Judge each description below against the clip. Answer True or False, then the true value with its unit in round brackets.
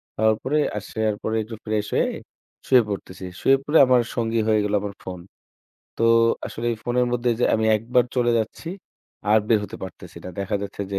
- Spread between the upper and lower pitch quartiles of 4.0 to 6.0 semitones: False (2.8 semitones)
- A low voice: True (110 Hz)